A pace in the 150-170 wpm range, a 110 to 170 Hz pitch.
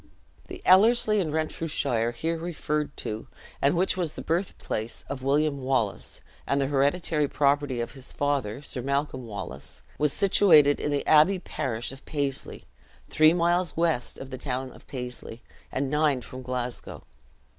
Yes: average, 155 wpm; medium, 140 Hz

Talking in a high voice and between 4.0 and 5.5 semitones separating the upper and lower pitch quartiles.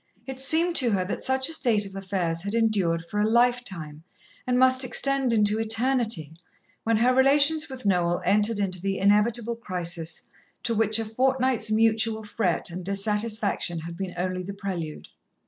Yes: high, 215 Hz; average, 4.7 semitones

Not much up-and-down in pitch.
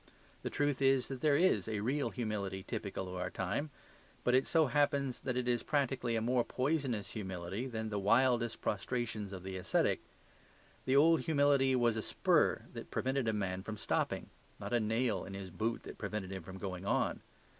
No: average, 5.1 semitones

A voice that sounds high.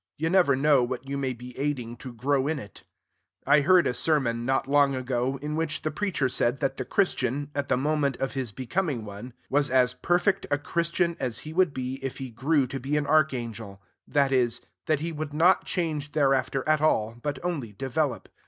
No: medium, 140 Hz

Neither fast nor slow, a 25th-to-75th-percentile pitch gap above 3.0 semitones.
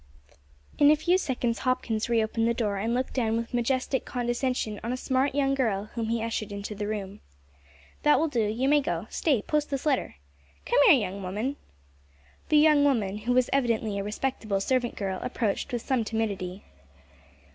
Yes: average, 180 wpm; average, 3.8 semitones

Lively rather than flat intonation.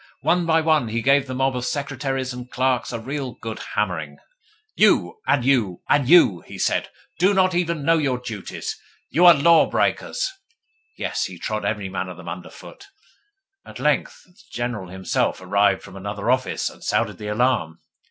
Yes: wide, 6.1 semitones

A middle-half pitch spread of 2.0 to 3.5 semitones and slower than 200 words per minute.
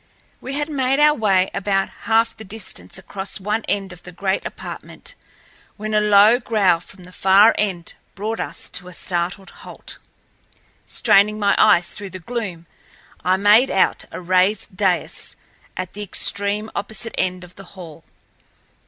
Yes: average, 2.7 semitones; average, 160 wpm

